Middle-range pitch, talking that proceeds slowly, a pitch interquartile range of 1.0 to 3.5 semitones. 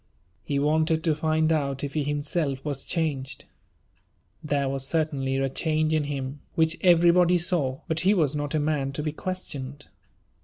No: medium, 150 Hz; average, 165 wpm; narrow, 2.5 semitones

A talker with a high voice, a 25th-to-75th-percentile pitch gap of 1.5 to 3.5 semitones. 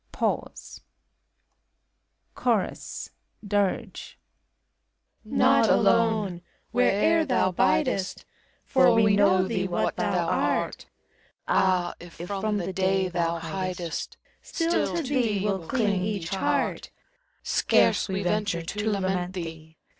Yes: high, 195 Hz; average, 3.0 semitones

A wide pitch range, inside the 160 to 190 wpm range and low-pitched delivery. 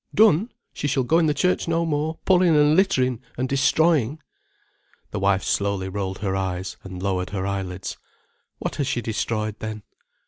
Yes: wide, 8.2 semitones; average, 170 wpm; low, 120 Hz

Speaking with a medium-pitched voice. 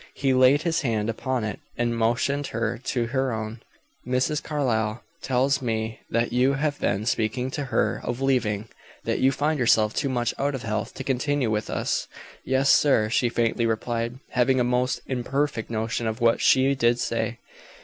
No: low, 125 Hz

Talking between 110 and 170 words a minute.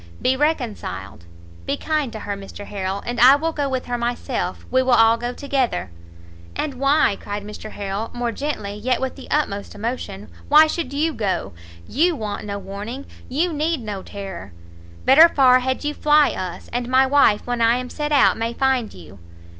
No: average, 185 wpm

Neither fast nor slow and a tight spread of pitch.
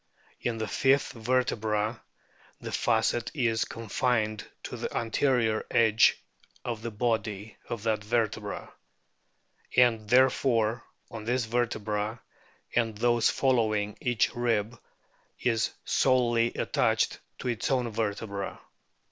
No: slow, 110 wpm; narrow, 2.0 semitones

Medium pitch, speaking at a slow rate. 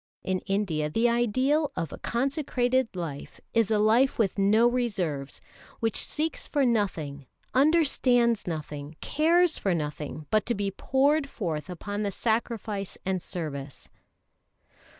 No: high, 215 Hz; slow, 130 wpm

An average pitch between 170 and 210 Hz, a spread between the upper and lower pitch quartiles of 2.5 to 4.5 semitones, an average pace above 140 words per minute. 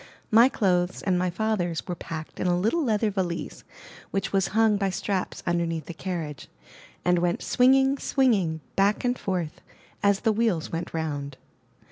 Yes: medium, 185 Hz; average, 4.1 semitones; average, 165 wpm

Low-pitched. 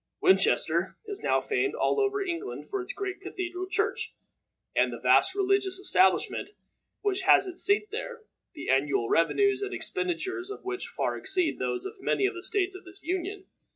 No: very high, 385 Hz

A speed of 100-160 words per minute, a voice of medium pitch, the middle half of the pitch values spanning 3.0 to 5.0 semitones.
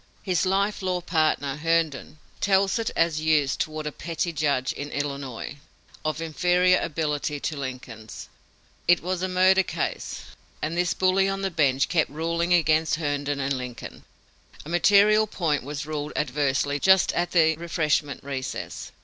Yes: average, 150 wpm; medium, 160 Hz; average, 3.8 semitones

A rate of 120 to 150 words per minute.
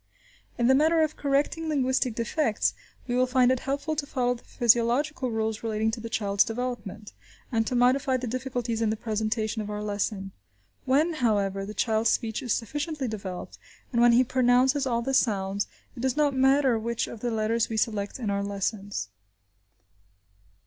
No: average, 175 wpm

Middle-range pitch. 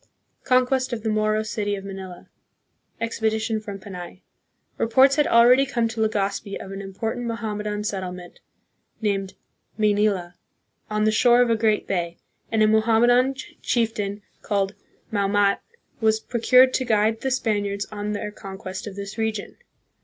No: high, 215 Hz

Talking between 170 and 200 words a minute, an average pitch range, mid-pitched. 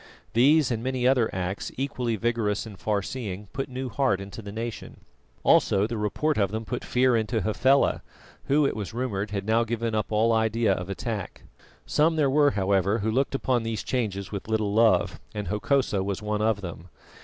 No: average, 190 wpm; average, 3.7 semitones; low, 110 Hz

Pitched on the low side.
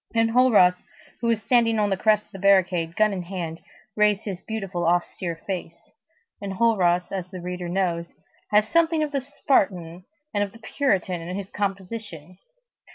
No: high, 195 Hz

